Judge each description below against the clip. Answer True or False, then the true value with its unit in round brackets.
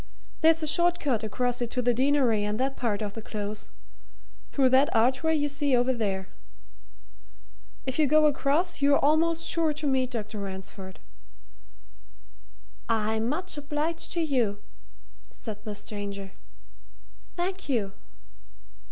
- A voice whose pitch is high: True (260 Hz)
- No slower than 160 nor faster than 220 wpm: False (135 wpm)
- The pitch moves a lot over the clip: True (5.9 semitones)